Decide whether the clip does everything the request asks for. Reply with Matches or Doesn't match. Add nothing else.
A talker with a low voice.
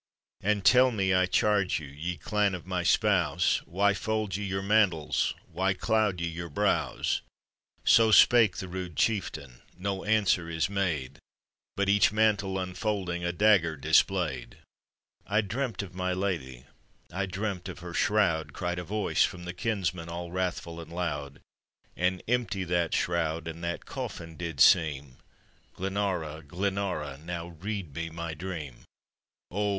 Matches